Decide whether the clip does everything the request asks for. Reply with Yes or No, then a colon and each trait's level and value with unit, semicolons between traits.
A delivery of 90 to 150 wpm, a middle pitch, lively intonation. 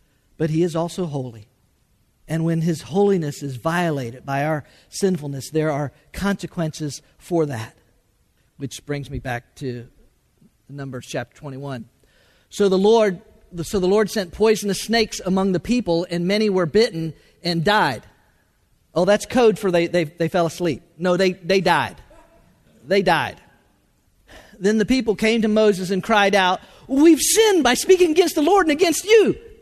No: average, 160 wpm; medium, 175 Hz; wide, 6.4 semitones